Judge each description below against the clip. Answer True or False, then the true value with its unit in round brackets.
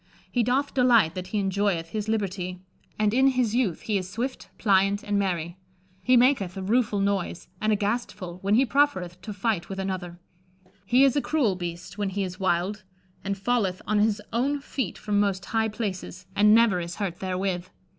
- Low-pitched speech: False (200 Hz)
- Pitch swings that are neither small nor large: True (3.8 semitones)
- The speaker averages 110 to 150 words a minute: False (190 wpm)